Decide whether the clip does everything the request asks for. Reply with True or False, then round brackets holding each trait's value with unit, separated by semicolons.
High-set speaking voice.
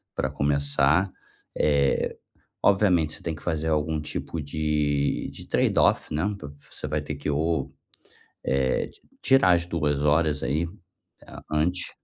False (75 Hz)